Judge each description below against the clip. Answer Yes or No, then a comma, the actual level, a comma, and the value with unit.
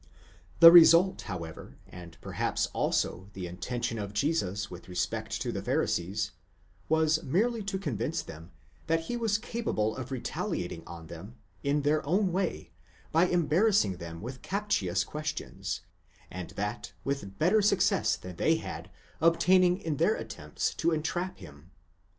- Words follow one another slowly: No, average, 145 wpm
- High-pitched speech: No, medium, 145 Hz